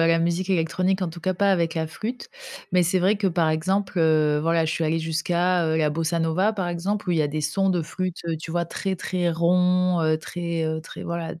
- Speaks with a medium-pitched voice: Yes, medium, 170 Hz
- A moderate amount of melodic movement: No, narrow, 2.2 semitones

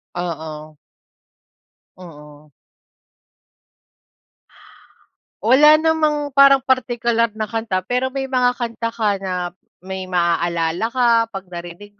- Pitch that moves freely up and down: Yes, wide, 6.6 semitones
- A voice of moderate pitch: No, high, 220 Hz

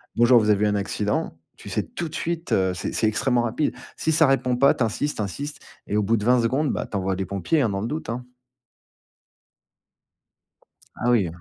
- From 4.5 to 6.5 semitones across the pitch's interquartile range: Yes, average, 5.1 semitones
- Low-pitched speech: Yes, low, 120 Hz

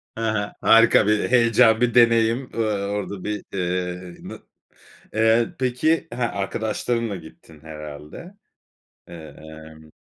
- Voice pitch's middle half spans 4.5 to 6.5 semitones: Yes, average, 5.2 semitones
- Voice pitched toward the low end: Yes, low, 105 Hz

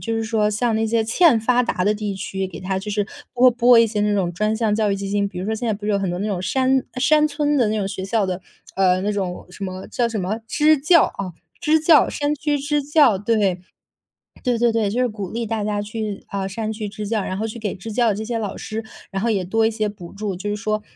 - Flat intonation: No, average, 3.0 semitones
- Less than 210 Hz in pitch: No, high, 215 Hz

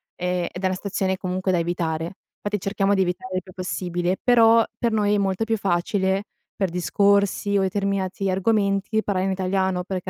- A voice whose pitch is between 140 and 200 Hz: Yes, high, 190 Hz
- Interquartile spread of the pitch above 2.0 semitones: No, narrow, 1.7 semitones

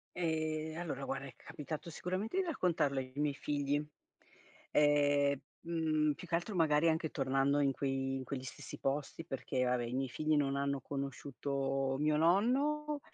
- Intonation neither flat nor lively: Yes, average, 3.0 semitones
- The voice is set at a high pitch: No, medium, 145 Hz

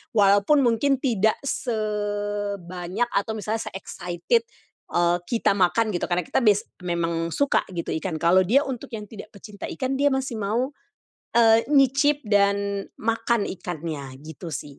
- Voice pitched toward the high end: Yes, high, 205 Hz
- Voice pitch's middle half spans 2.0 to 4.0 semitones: No, average, 4.9 semitones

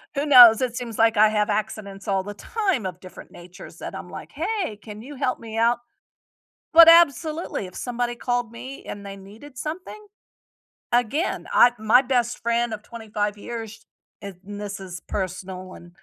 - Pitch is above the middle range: Yes, high, 225 Hz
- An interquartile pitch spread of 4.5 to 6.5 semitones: No, average, 3.7 semitones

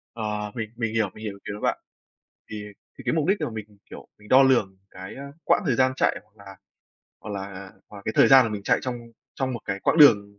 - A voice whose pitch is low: Yes, low, 110 Hz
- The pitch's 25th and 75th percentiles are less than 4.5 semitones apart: Yes, average, 4.1 semitones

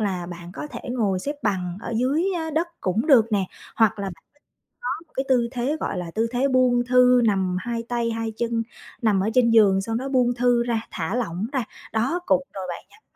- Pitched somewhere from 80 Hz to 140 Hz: No, high, 230 Hz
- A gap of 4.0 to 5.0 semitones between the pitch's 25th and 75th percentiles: Yes, average, 4.3 semitones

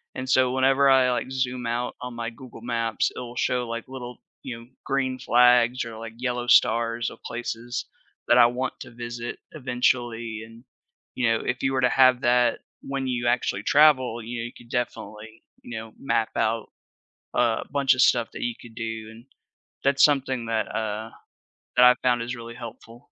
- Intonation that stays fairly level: Yes, narrow, 1.7 semitones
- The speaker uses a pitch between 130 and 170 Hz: No, low, 120 Hz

